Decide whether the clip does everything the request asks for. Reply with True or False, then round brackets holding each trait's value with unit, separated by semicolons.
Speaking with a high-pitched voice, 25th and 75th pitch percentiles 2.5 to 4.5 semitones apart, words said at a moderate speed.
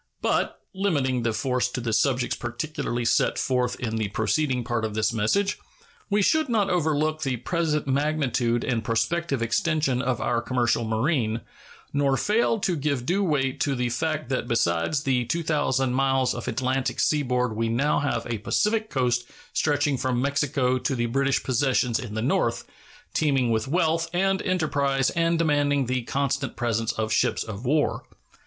False (135 Hz; 4.2 semitones; 165 wpm)